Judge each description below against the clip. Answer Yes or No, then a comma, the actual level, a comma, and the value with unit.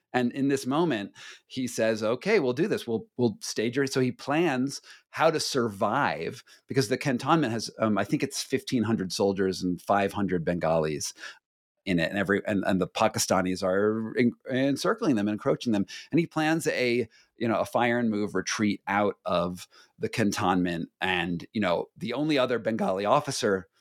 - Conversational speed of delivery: Yes, average, 175 wpm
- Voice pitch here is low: Yes, low, 110 Hz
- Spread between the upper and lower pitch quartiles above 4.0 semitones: Yes, wide, 5.4 semitones